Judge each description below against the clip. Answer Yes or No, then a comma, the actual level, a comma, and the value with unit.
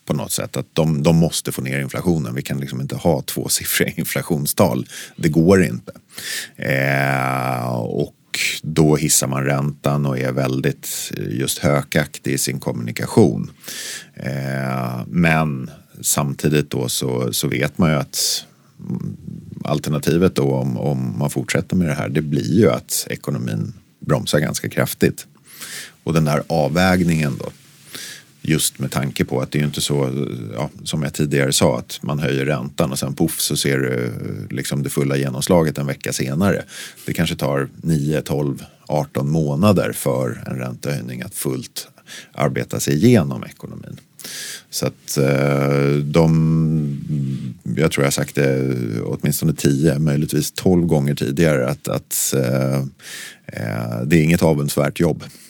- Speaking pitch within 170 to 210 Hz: No, very low, 70 Hz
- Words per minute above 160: No, average, 150 wpm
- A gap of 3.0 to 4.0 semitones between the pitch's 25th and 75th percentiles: No, narrow, 2.4 semitones